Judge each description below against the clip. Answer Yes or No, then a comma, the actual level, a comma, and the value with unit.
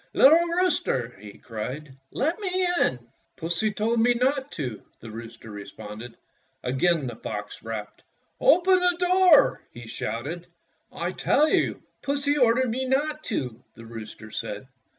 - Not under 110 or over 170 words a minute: Yes, average, 145 wpm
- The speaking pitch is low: No, medium, 175 Hz